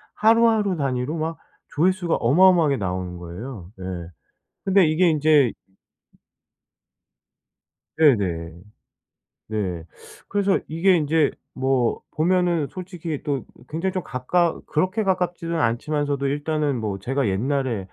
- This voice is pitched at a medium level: Yes, medium, 150 Hz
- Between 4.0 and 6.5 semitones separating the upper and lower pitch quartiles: Yes, wide, 6.2 semitones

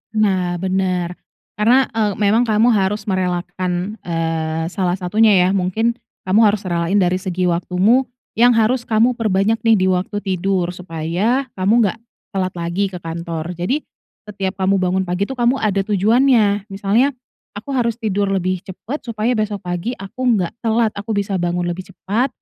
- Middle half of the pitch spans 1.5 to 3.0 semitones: No, average, 3.6 semitones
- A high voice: Yes, high, 195 Hz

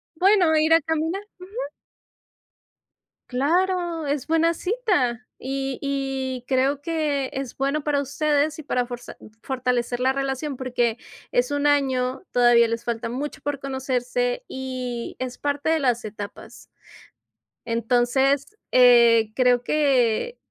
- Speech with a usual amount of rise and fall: Yes, average, 3.6 semitones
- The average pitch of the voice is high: Yes, very high, 270 Hz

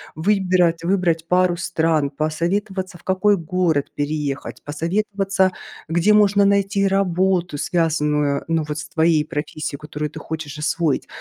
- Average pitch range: Yes, average, 3.6 semitones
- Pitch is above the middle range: No, medium, 170 Hz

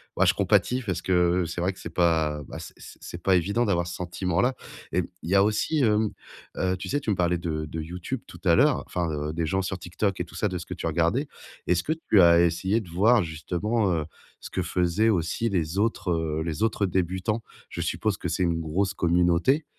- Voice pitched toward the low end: Yes, very low, 90 Hz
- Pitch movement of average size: Yes, average, 3.3 semitones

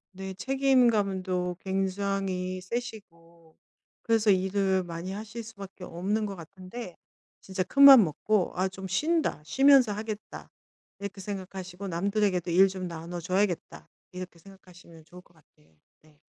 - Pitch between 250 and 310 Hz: No, high, 190 Hz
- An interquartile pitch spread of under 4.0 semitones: Yes, narrow, 2.5 semitones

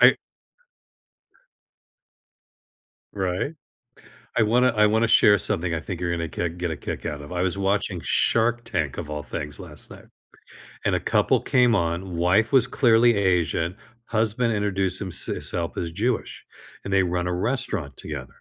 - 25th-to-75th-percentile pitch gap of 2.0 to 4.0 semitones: No, average, 4.7 semitones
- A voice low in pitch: Yes, very low, 95 Hz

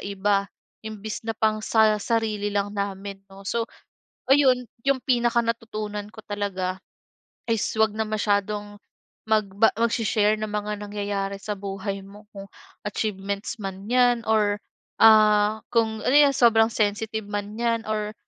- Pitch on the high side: Yes, high, 210 Hz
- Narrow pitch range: Yes, narrow, 1.7 semitones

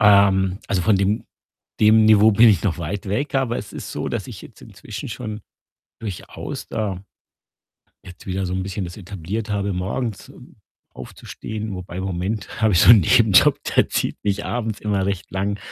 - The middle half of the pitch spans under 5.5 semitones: Yes, narrow, 2.4 semitones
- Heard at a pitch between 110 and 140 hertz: No, low, 100 Hz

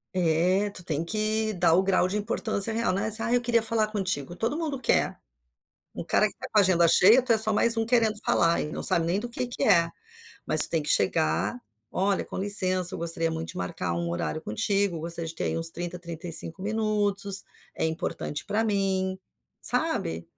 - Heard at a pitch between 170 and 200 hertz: Yes, high, 190 Hz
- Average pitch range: Yes, average, 4.5 semitones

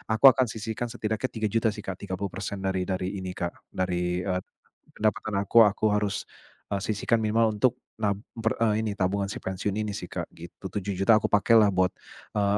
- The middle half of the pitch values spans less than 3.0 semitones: Yes, narrow, 2.4 semitones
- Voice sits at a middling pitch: No, low, 100 Hz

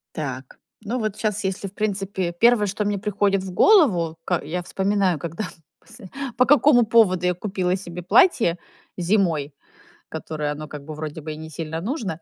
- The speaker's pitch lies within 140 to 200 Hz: Yes, medium, 185 Hz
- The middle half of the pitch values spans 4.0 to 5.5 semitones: Yes, average, 4.5 semitones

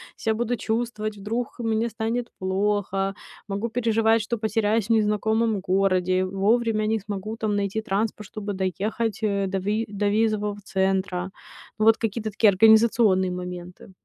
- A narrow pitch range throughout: Yes, narrow, 2.3 semitones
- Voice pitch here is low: No, high, 210 Hz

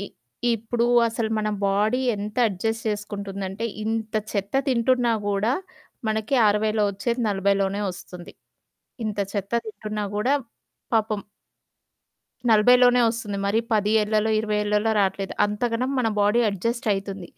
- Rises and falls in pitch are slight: Yes, narrow, 2.1 semitones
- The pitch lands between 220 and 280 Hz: No, high, 210 Hz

